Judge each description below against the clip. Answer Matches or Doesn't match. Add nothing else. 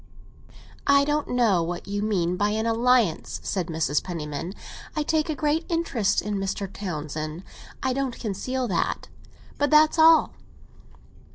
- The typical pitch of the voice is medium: Doesn't match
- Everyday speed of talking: Matches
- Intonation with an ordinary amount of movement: Doesn't match